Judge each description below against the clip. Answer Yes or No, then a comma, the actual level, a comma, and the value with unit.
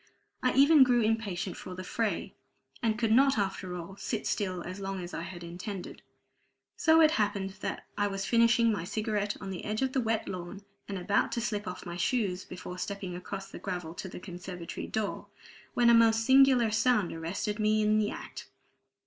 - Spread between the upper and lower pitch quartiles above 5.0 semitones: No, average, 3.8 semitones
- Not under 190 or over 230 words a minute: Yes, average, 195 wpm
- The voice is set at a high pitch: Yes, high, 205 Hz